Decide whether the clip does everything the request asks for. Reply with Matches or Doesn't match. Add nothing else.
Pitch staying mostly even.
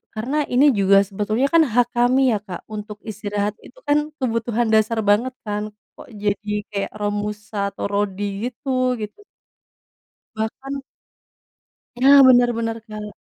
Doesn't match